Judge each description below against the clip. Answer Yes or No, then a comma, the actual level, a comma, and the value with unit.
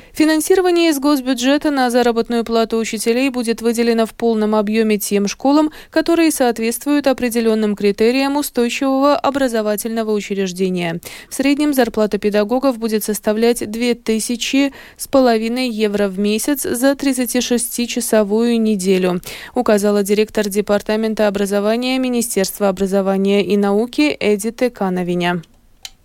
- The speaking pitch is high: Yes, high, 230 Hz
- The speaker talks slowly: Yes, slow, 105 wpm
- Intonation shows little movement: No, average, 3.6 semitones